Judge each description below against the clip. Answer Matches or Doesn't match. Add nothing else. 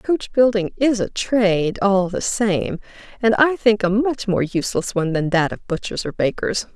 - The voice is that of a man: Doesn't match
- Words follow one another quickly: Doesn't match